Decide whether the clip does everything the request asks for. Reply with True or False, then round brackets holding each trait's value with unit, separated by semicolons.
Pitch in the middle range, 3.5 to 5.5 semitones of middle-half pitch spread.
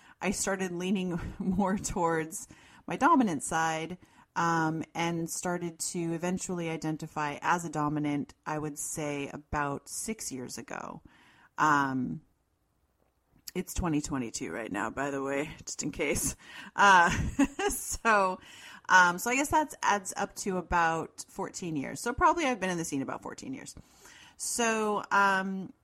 True (170 Hz; 4.5 semitones)